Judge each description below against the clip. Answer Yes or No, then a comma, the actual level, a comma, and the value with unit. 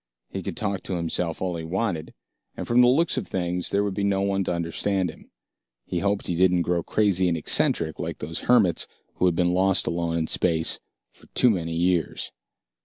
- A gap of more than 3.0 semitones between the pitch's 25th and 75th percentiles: No, average, 2.7 semitones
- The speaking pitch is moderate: No, very low, 90 Hz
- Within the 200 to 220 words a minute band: Yes, fast, 205 wpm